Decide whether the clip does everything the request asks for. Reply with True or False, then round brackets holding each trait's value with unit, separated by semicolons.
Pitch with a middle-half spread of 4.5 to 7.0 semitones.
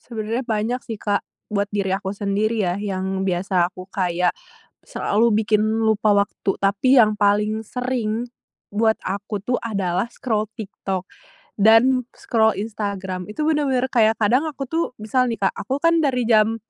False (2.7 semitones)